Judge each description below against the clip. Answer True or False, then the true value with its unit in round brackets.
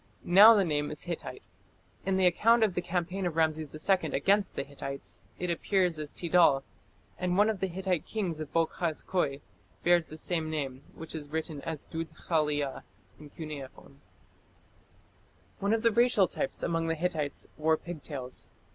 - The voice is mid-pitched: True (165 Hz)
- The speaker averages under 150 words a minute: False (165 wpm)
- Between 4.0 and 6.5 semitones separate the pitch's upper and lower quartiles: False (3.4 semitones)